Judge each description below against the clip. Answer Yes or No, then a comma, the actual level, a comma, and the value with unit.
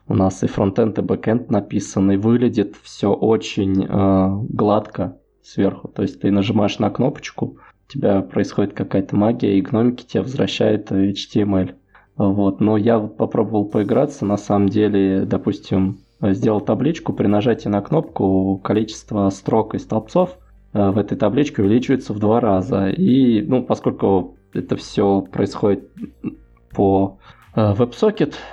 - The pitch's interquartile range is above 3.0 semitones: No, narrow, 2.4 semitones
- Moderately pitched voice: No, low, 105 Hz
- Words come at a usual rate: Yes, average, 130 wpm